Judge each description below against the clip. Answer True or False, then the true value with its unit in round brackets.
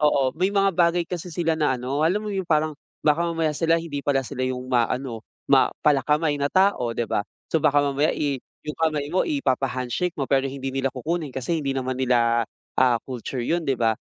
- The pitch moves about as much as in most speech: True (4.1 semitones)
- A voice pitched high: False (145 Hz)